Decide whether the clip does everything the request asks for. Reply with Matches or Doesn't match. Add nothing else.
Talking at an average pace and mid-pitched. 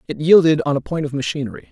Doesn't match